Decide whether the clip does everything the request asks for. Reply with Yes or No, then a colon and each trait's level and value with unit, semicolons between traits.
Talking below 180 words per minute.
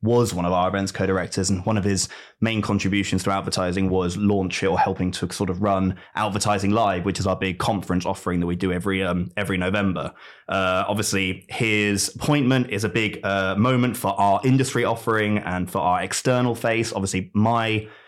No: average, 190 wpm